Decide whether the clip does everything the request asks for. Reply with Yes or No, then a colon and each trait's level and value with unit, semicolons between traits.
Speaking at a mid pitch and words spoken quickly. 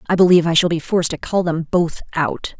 Yes: medium, 170 Hz; fast, 255 wpm